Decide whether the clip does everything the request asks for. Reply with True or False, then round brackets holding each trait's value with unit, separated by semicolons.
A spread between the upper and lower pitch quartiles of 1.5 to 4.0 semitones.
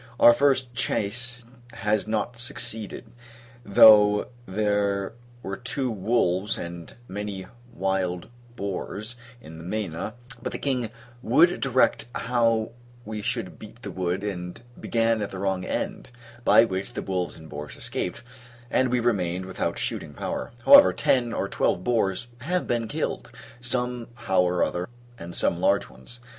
False (4.4 semitones)